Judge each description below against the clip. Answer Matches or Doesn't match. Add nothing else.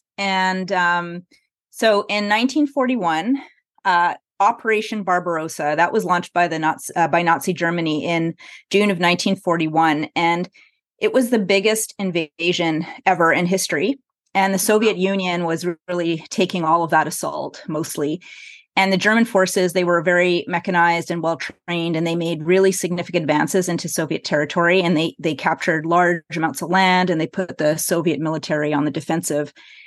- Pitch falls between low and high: Matches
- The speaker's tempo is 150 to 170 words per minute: Matches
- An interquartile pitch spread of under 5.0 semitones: Matches